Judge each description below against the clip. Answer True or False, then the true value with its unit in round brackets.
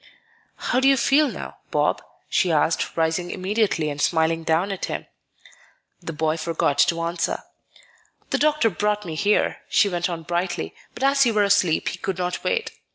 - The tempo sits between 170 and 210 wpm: True (175 wpm)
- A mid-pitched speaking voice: True (180 Hz)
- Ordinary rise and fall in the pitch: True (4.3 semitones)